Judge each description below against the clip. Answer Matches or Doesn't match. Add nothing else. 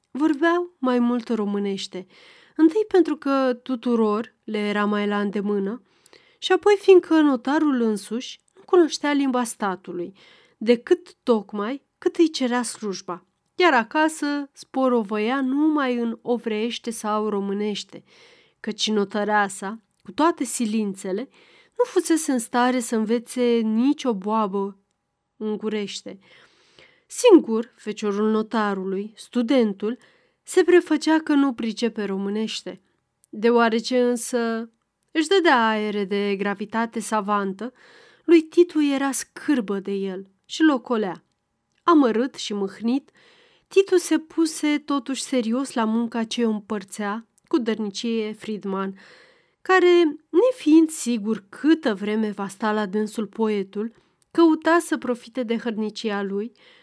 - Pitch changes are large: Matches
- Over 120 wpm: Doesn't match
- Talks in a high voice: Matches